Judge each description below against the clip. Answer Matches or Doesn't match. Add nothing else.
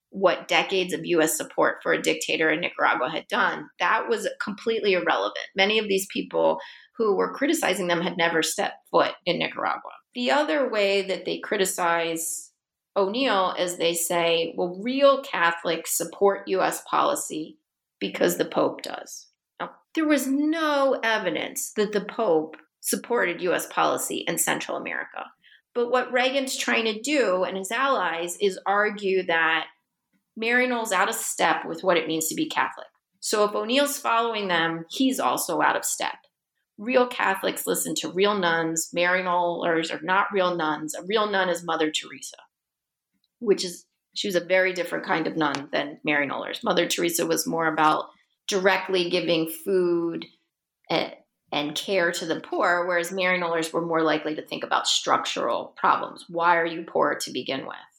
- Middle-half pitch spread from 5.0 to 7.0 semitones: Matches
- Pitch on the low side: Doesn't match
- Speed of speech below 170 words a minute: Matches